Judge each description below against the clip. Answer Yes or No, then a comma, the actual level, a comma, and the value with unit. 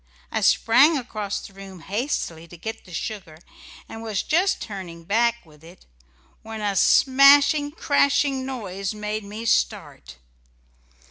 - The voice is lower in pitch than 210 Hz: No, high, 215 Hz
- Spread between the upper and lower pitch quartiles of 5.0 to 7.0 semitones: Yes, wide, 5.6 semitones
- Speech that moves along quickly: No, slow, 135 wpm